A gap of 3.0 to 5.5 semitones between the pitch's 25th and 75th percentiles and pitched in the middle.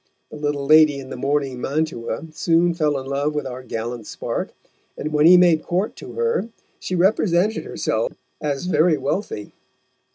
Yes: average, 4.1 semitones; medium, 150 Hz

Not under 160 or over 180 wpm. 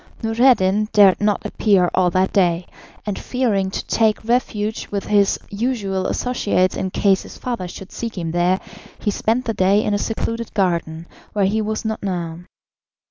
Yes: average, 170 wpm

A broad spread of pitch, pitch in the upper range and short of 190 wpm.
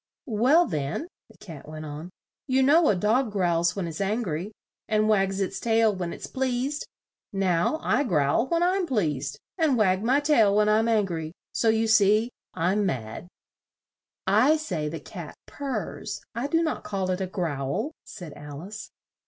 Yes: wide, 6.4 semitones; high, 205 Hz; average, 170 wpm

